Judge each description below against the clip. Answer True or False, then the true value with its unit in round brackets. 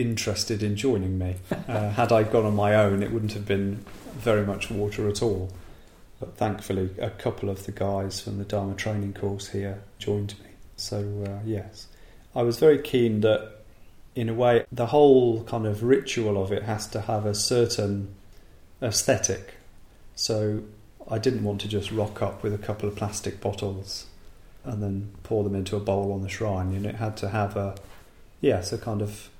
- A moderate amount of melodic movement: False (1.8 semitones)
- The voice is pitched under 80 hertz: False (105 Hz)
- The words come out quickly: False (190 wpm)